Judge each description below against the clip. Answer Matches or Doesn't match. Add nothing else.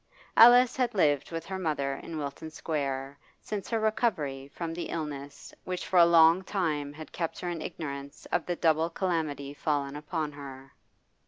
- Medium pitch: Matches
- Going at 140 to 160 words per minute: Doesn't match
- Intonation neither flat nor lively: Matches